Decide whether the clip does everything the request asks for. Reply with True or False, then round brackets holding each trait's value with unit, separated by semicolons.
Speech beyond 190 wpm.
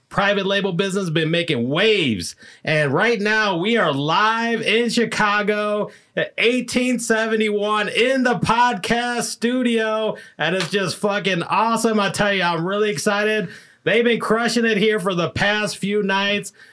False (145 wpm)